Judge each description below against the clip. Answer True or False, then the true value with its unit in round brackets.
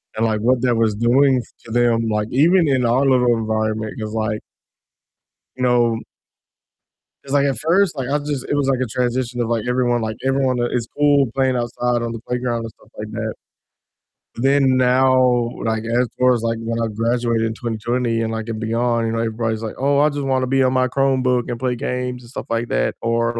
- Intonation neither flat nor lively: False (2.2 semitones)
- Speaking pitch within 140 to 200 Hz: False (120 Hz)